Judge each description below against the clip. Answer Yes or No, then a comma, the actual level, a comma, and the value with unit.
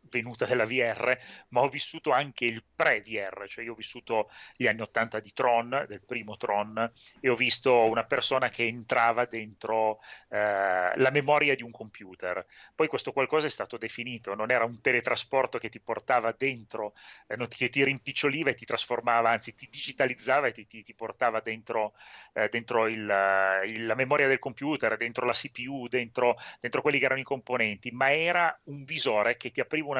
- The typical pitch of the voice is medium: No, low, 120 Hz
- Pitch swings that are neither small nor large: Yes, average, 3.1 semitones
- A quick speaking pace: Yes, fast, 180 wpm